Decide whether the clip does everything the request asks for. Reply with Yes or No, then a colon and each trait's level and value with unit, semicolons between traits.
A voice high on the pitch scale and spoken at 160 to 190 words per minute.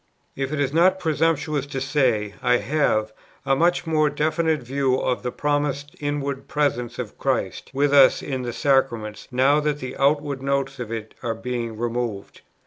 No: low, 135 Hz; average, 170 wpm